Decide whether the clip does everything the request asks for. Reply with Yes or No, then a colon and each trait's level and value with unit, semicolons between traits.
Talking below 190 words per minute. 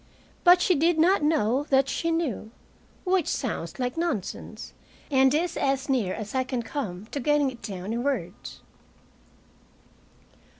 Yes: average, 145 wpm